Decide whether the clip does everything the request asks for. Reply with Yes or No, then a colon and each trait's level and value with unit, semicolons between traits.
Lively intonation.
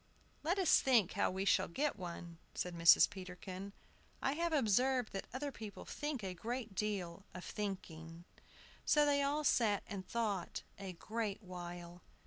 Yes: wide, 6.3 semitones